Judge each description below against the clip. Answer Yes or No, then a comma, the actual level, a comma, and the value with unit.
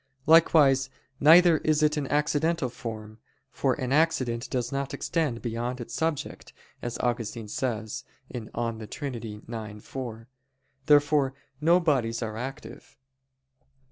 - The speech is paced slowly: Yes, slow, 120 wpm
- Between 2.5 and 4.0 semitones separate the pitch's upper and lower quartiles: No, average, 4.4 semitones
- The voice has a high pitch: No, low, 130 Hz